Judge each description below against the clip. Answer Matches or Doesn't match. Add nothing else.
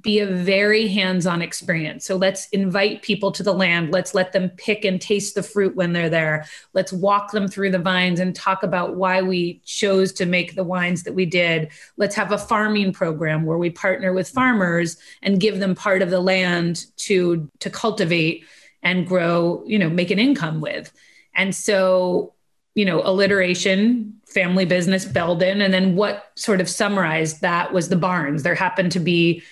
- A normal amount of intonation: Doesn't match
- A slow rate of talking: Doesn't match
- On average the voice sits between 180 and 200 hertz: Matches